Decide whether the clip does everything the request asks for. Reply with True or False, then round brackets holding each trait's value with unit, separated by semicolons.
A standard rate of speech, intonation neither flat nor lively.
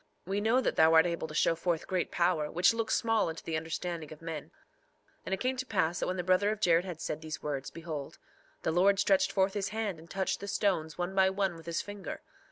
False (250 wpm; 3.5 semitones)